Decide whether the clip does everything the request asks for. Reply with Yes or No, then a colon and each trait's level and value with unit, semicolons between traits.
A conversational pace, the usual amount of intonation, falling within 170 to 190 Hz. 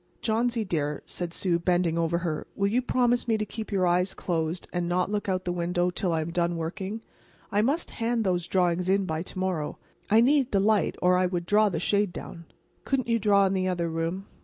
No: fast, 225 wpm; average, 3.5 semitones; medium, 185 Hz